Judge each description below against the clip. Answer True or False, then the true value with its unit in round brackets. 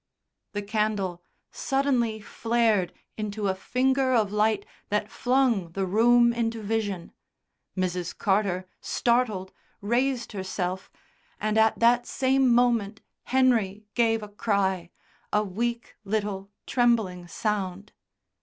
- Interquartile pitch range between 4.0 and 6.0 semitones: False (3.4 semitones)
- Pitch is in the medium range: False (215 Hz)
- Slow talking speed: True (110 wpm)